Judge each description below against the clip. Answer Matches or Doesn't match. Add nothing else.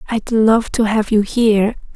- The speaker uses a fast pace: Doesn't match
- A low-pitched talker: Doesn't match